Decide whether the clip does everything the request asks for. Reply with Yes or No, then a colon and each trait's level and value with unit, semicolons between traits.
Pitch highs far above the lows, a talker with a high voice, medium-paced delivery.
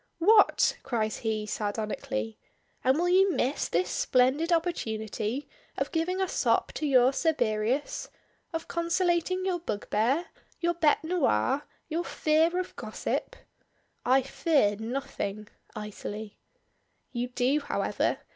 No: wide, 7.6 semitones; very high, 270 Hz; slow, 120 wpm